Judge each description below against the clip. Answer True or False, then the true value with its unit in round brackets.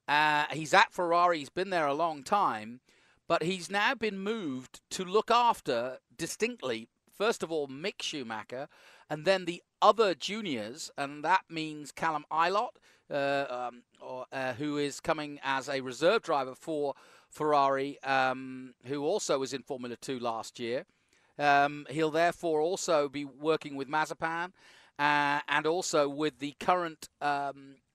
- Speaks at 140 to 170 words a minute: True (150 wpm)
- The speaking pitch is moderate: True (150 Hz)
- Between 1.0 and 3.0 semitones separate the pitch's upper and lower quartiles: False (3.7 semitones)